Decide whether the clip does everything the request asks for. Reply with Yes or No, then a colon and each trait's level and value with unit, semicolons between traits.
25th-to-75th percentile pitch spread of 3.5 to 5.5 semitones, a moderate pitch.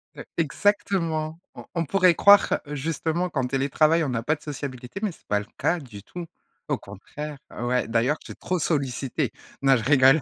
Yes: average, 4.6 semitones; medium, 150 Hz